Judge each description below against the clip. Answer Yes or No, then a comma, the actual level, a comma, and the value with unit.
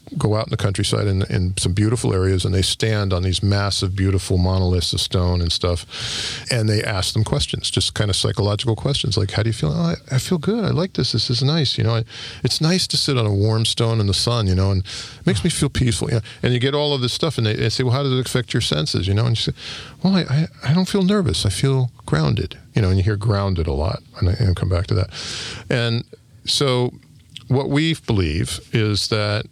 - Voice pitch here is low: Yes, low, 115 Hz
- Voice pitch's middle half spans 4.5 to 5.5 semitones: Yes, average, 4.9 semitones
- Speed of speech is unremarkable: No, fast, 255 wpm